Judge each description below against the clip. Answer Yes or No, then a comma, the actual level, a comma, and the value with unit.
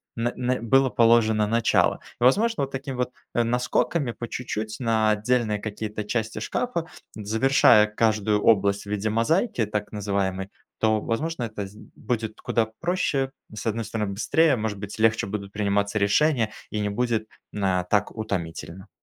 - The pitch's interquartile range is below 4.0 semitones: Yes, average, 2.9 semitones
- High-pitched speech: No, low, 110 Hz